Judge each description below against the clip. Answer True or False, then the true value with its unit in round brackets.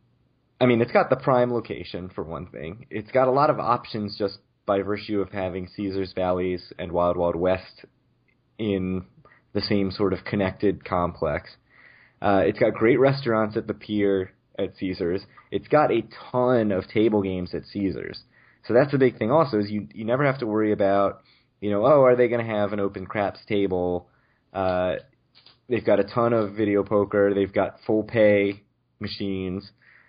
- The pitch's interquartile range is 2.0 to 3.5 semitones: True (3.1 semitones)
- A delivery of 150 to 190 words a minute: True (185 wpm)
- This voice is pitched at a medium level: False (100 Hz)